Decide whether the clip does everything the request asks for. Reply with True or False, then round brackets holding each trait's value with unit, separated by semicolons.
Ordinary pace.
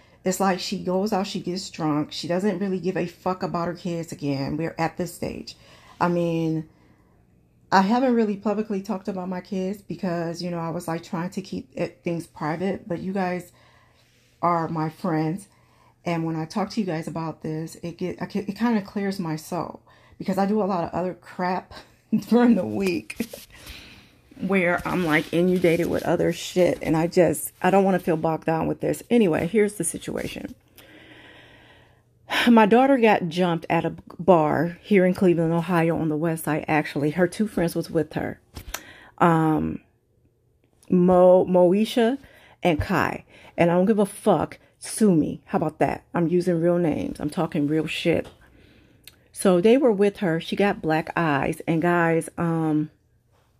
True (180 wpm)